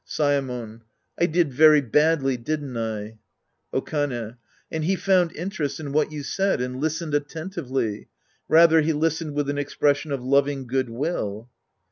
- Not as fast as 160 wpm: Yes, average, 145 wpm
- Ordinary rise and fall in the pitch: Yes, average, 3.8 semitones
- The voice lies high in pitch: No, medium, 145 Hz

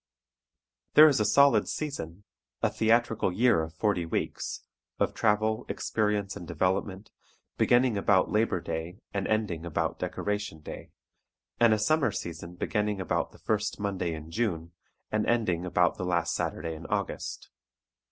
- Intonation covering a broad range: No, average, 4.2 semitones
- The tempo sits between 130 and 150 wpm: Yes, average, 145 wpm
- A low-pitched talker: Yes, low, 100 Hz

